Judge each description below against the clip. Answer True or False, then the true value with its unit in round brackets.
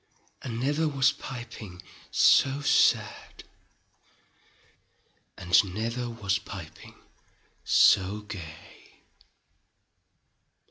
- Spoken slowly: True (65 wpm)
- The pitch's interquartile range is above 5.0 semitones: True (5.6 semitones)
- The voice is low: True (110 Hz)